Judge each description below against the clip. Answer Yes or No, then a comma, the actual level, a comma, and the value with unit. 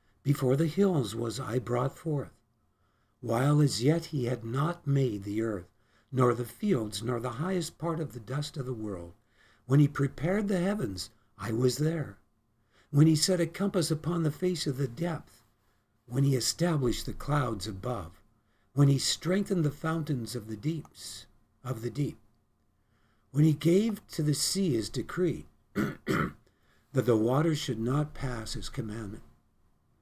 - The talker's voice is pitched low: Yes, low, 130 Hz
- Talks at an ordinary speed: Yes, average, 160 wpm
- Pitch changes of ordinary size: No, wide, 5.8 semitones